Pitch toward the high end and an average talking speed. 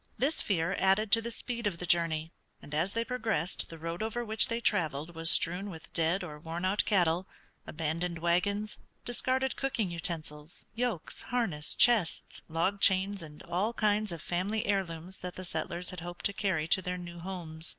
No: medium, 180 Hz; average, 180 wpm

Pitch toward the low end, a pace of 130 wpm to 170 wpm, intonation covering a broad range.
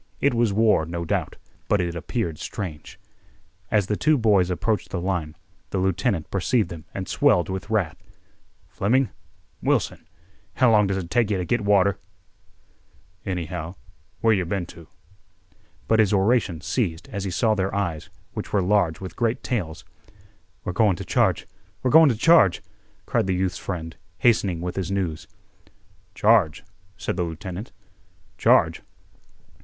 No: very low, 95 Hz; average, 145 wpm; average, 3.7 semitones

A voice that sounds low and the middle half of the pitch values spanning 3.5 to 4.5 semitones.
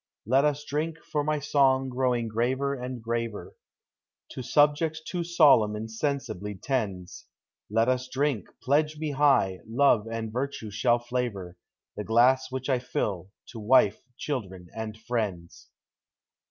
Yes: low, 125 Hz; average, 4.2 semitones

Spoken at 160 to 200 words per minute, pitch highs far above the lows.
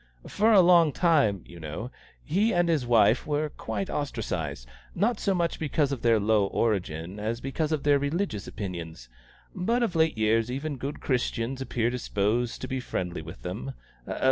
Yes: average, 170 wpm; wide, 7.2 semitones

